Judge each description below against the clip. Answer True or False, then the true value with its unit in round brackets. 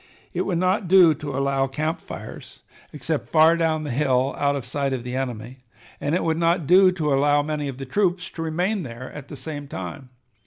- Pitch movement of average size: True (3.6 semitones)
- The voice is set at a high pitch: False (145 Hz)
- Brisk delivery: True (210 wpm)